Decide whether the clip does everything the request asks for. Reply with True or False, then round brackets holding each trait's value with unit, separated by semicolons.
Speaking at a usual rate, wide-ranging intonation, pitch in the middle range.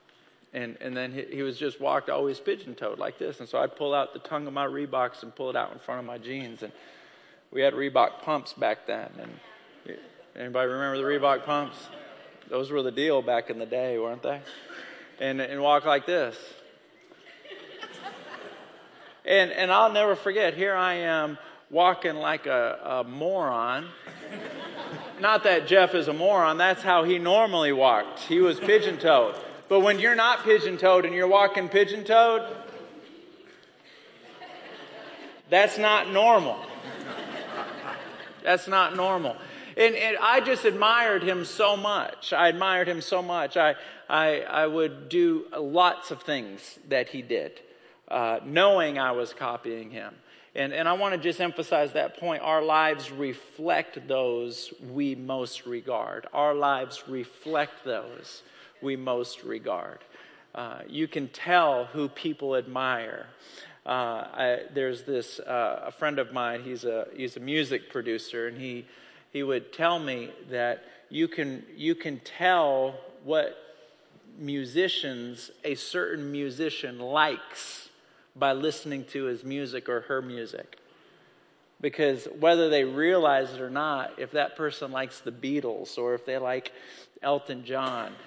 True (150 wpm; 5.9 semitones; 150 Hz)